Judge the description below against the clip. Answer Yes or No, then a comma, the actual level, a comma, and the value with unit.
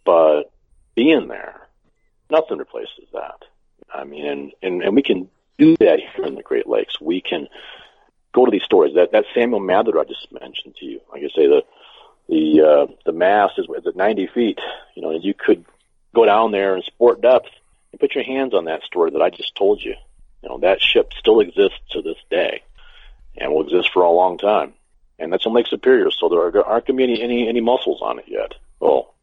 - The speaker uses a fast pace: Yes, fast, 215 wpm